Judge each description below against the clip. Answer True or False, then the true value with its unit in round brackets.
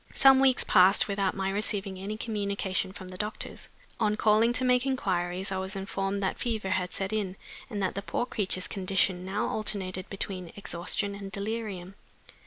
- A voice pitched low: False (195 Hz)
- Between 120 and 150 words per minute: False (175 wpm)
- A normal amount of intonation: False (2.2 semitones)